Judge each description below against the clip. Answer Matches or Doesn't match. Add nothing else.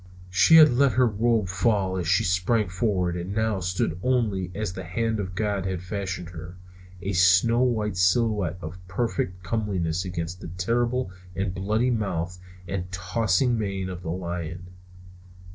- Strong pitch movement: Doesn't match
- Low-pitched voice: Matches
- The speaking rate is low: Doesn't match